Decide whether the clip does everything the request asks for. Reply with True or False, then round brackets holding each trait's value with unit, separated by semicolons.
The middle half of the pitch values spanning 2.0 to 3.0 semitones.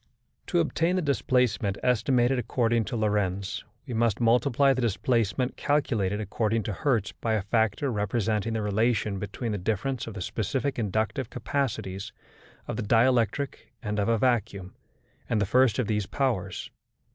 False (3.4 semitones)